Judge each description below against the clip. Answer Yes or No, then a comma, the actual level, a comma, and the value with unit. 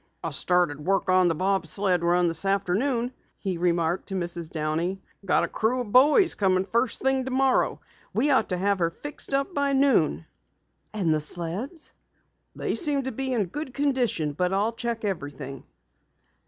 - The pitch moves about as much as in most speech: No, wide, 7.0 semitones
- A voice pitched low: No, high, 195 Hz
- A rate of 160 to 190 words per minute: Yes, average, 170 wpm